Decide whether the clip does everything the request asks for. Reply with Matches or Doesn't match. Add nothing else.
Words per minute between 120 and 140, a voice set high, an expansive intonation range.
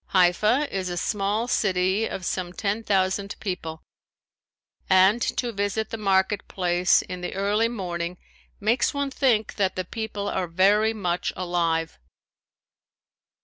Doesn't match